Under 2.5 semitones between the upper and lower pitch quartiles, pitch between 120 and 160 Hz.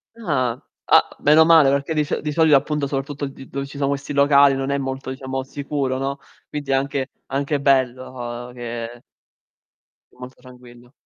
Yes: narrow, 1.7 semitones; low, 135 Hz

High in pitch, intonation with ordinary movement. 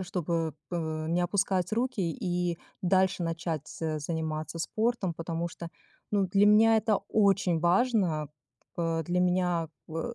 No: medium, 175 Hz; average, 3.0 semitones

